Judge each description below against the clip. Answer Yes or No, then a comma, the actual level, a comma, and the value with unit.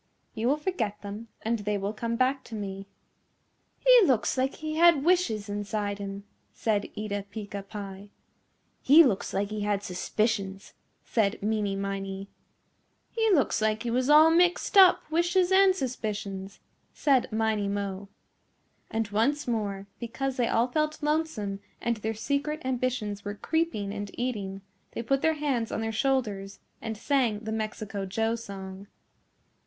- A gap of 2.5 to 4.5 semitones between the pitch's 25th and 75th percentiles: No, average, 5.1 semitones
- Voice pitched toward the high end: Yes, high, 220 Hz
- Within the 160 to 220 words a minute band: No, average, 150 wpm